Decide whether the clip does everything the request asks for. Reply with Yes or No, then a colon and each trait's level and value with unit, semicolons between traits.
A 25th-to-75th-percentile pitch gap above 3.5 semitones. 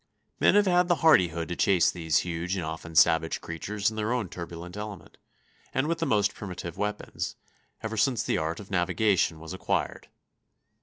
Yes: average, 4.6 semitones